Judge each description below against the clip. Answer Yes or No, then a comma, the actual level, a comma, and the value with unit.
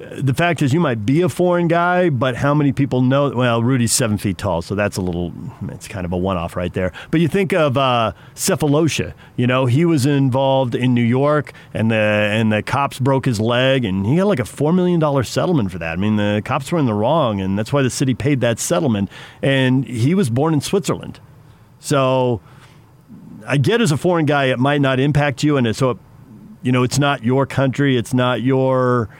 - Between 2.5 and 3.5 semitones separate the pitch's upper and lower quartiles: No, average, 3.9 semitones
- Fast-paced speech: Yes, fast, 220 wpm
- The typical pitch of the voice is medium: No, low, 130 Hz